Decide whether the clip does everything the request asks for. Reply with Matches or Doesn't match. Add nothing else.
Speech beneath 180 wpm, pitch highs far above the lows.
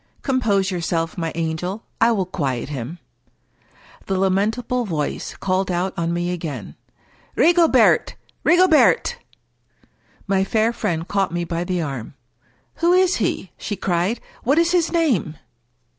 Matches